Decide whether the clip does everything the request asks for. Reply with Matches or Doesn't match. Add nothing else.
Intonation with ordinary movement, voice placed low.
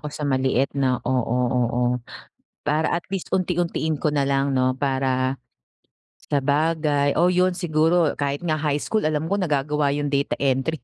Doesn't match